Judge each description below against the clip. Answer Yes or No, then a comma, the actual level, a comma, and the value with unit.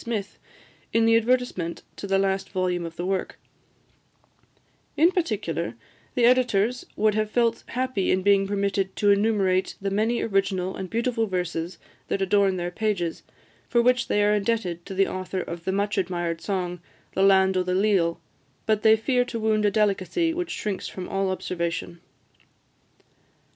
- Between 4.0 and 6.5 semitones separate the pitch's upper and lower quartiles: No, average, 3.1 semitones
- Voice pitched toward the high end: Yes, high, 195 Hz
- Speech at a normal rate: Yes, average, 165 wpm